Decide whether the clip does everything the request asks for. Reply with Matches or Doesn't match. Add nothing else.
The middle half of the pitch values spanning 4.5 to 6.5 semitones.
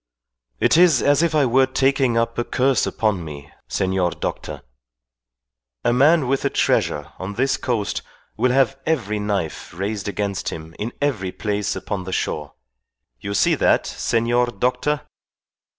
Matches